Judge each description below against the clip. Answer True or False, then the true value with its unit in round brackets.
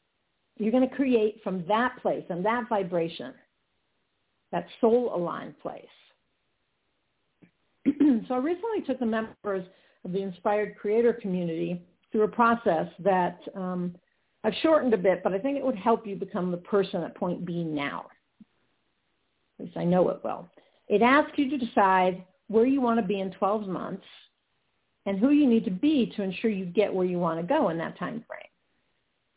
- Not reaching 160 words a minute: False (175 wpm)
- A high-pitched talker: True (210 Hz)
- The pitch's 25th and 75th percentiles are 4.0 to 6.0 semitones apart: True (4.4 semitones)